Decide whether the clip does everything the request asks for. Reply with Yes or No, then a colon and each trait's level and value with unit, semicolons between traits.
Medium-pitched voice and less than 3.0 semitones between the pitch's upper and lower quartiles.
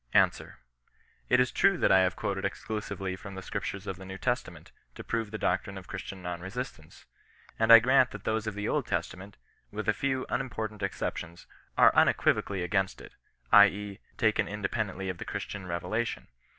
No: low, 100 Hz; narrow, 2.6 semitones